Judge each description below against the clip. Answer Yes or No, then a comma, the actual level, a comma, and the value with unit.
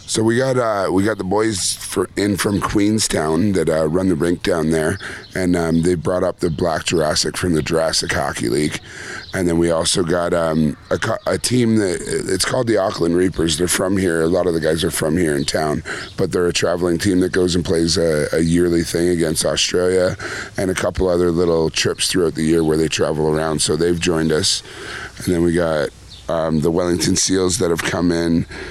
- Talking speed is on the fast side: Yes, fast, 215 wpm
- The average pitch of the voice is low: Yes, very low, 85 Hz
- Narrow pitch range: Yes, narrow, 2.3 semitones